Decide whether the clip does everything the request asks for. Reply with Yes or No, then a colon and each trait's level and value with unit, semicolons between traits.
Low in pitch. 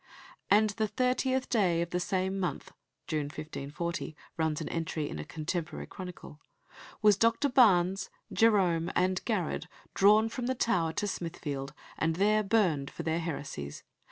No: medium, 180 Hz